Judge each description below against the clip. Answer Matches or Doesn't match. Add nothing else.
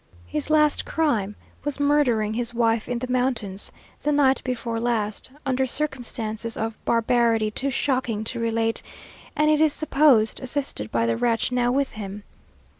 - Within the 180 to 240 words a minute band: Doesn't match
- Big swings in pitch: Doesn't match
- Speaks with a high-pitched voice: Matches